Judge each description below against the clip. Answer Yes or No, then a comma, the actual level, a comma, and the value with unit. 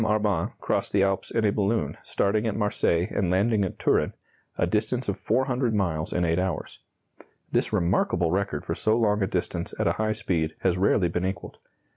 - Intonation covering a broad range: No, average, 3.4 semitones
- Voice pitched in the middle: No, low, 100 Hz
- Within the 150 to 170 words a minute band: No, average, 190 wpm